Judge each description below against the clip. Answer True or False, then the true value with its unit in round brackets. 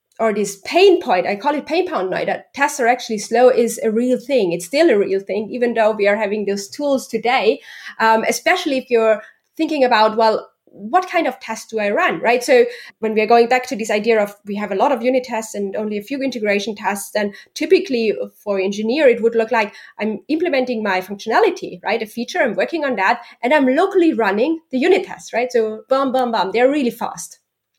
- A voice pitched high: True (230 Hz)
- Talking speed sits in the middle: False (225 wpm)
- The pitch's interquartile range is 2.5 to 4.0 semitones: False (4.4 semitones)